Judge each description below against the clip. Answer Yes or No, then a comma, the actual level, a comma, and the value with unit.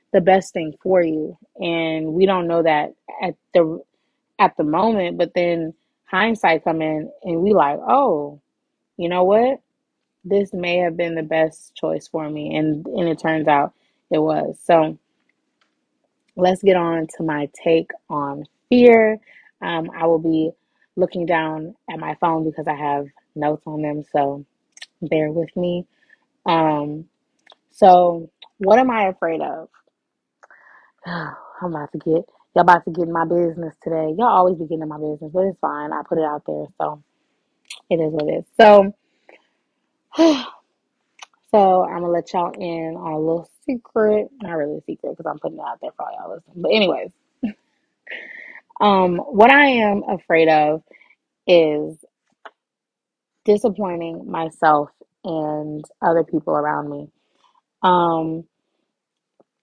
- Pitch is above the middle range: No, medium, 170 Hz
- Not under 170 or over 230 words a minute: No, average, 155 wpm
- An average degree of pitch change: Yes, average, 4.6 semitones